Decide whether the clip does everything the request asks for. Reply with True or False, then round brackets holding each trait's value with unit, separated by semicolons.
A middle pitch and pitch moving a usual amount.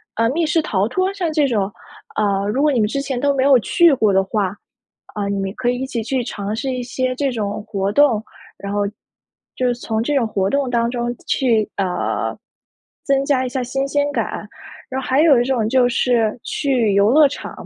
False (245 Hz; 4.5 semitones)